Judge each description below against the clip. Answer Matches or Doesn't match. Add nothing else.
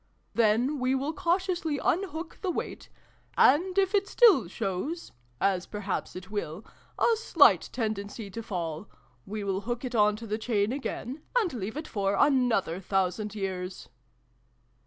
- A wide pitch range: Matches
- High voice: Matches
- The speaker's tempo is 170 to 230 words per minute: Doesn't match